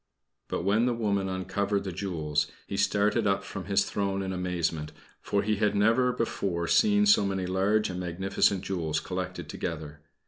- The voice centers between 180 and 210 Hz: No, very low, 95 Hz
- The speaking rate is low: No, average, 170 wpm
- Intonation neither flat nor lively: No, narrow, 2.3 semitones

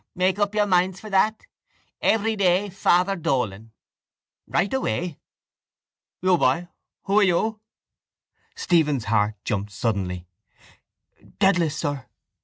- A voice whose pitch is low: No, medium, 175 Hz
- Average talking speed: No, slow, 110 wpm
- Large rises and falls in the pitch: Yes, wide, 7.6 semitones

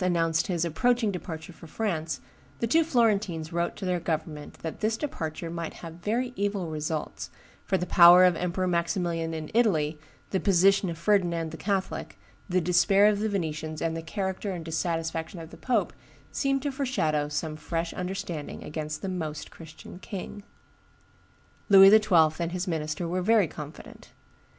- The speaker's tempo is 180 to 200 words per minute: No, average, 165 wpm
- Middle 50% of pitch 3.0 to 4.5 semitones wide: Yes, average, 3.5 semitones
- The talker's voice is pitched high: No, medium, 175 Hz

